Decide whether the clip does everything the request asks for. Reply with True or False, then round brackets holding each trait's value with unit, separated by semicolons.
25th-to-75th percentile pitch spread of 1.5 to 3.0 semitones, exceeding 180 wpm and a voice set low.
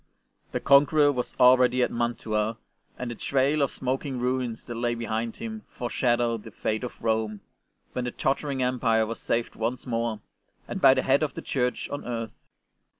True (2.4 semitones; 190 wpm; 125 Hz)